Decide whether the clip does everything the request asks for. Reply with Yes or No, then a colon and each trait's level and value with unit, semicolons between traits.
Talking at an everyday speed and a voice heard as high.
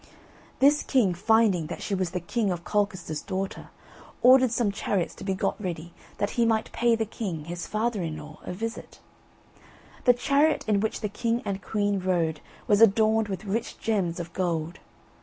Yes: average, 180 wpm; high, 200 Hz